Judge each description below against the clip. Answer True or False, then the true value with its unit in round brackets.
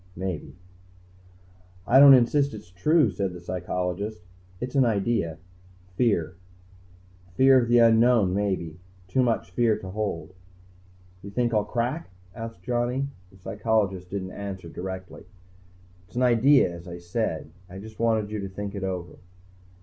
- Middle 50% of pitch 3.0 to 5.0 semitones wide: True (4.5 semitones)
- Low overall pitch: True (105 Hz)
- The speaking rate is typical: True (145 wpm)